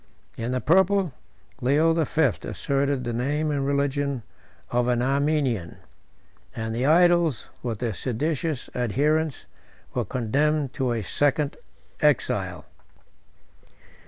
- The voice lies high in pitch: No, medium, 140 Hz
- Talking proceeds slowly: Yes, slow, 115 wpm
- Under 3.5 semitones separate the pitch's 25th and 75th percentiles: No, average, 3.8 semitones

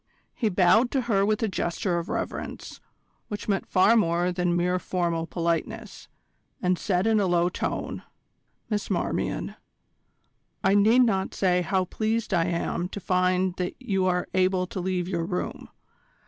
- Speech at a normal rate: Yes, average, 160 wpm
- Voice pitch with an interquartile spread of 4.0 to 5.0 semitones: No, narrow, 2.5 semitones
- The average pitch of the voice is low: No, medium, 185 Hz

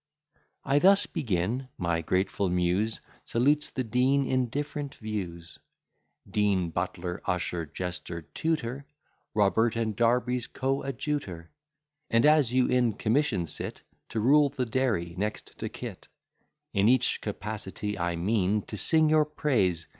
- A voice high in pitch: No, low, 110 Hz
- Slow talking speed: Yes, slow, 130 wpm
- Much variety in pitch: Yes, wide, 6.3 semitones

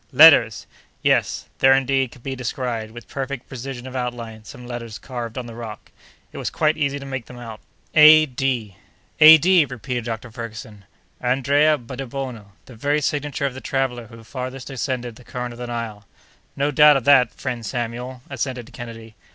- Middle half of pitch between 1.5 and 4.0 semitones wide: Yes, average, 2.7 semitones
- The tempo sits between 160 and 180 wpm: Yes, average, 170 wpm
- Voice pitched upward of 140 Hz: No, low, 125 Hz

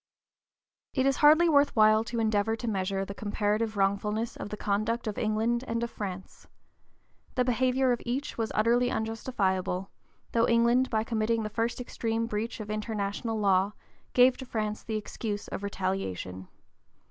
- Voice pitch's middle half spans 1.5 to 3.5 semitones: Yes, narrow, 2.4 semitones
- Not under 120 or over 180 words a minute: Yes, average, 160 wpm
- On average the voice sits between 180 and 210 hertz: No, high, 220 Hz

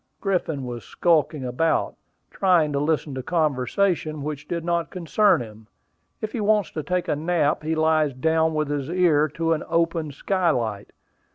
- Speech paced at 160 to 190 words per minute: Yes, average, 165 wpm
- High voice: No, medium, 160 Hz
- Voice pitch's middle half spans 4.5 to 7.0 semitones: No, average, 3.0 semitones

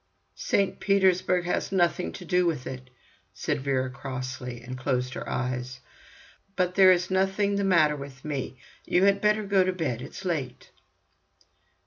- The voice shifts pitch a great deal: Yes, wide, 6.6 semitones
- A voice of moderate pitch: Yes, medium, 170 Hz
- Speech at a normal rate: Yes, average, 155 wpm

